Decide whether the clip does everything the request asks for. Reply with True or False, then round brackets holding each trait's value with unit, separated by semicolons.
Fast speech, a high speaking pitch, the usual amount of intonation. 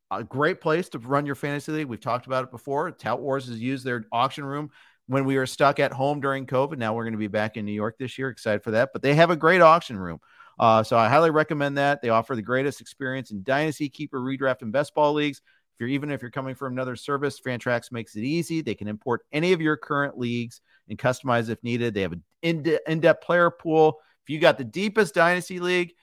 False (245 wpm; 135 Hz; 4.3 semitones)